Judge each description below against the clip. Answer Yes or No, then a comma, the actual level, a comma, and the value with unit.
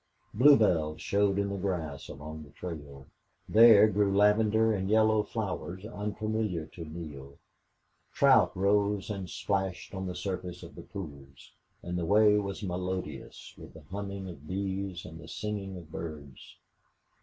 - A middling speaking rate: Yes, average, 145 wpm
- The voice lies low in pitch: Yes, very low, 95 Hz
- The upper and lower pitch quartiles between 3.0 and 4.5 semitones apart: Yes, average, 4.0 semitones